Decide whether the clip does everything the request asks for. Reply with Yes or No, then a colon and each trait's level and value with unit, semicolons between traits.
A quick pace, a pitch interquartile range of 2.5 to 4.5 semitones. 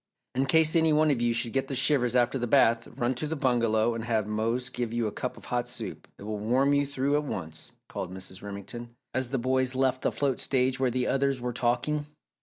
Yes: fast, 235 wpm; average, 2.8 semitones